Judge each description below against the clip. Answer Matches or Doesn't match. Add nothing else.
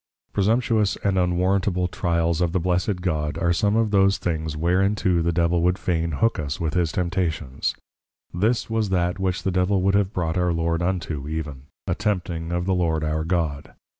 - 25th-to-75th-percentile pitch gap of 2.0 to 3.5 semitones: Matches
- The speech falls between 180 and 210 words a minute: Matches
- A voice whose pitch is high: Doesn't match